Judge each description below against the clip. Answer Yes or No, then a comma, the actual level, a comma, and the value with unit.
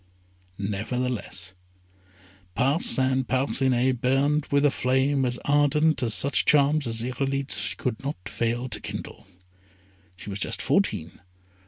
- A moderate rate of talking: No, slow, 120 wpm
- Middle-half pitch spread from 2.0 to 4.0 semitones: Yes, average, 2.8 semitones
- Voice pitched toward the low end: Yes, low, 130 Hz